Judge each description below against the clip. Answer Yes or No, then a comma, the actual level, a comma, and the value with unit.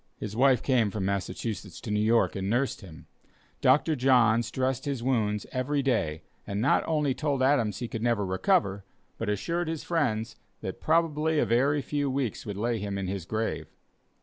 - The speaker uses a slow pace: No, average, 180 wpm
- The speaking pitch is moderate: No, low, 120 Hz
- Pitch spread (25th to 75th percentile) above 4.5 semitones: Yes, average, 5.2 semitones